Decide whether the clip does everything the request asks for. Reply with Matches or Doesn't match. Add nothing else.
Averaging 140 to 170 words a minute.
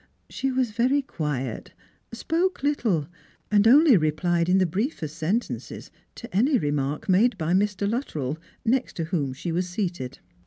Matches